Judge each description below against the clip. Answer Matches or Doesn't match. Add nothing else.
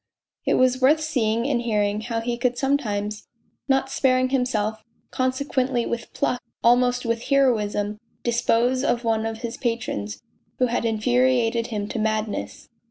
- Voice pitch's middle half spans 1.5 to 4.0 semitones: Matches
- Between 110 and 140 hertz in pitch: Doesn't match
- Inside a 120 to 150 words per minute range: Matches